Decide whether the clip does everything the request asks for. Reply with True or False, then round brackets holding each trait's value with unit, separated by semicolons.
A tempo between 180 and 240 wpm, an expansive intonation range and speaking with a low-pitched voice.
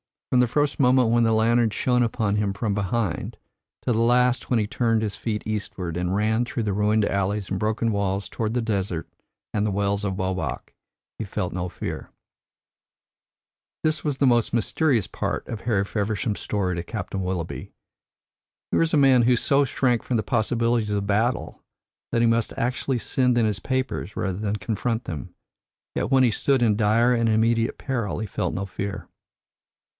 False (185 wpm; 3.1 semitones; 110 Hz)